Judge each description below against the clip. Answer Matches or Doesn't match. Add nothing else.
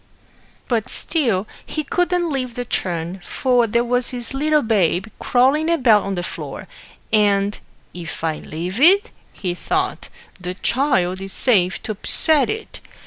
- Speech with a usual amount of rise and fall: Doesn't match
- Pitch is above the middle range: Matches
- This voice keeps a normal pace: Matches